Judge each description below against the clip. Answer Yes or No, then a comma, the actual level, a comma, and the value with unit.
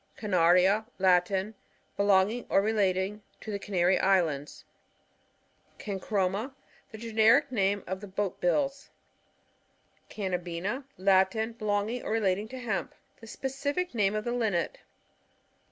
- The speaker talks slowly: Yes, slow, 120 wpm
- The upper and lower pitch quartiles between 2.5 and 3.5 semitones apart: Yes, average, 3.1 semitones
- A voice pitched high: Yes, high, 205 Hz